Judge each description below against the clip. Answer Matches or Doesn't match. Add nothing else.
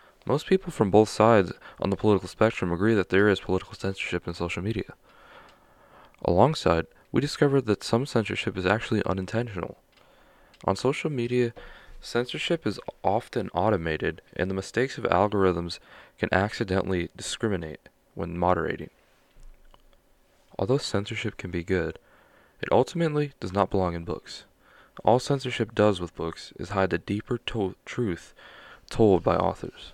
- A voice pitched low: Matches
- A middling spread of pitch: Matches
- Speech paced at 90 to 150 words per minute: Matches